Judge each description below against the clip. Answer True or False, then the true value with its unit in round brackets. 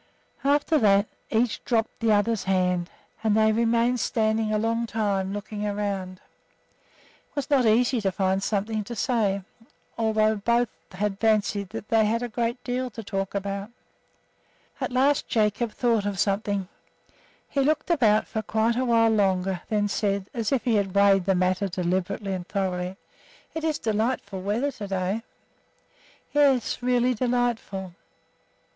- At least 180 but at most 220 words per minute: False (155 wpm)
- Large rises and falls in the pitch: False (3.1 semitones)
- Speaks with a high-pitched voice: True (215 Hz)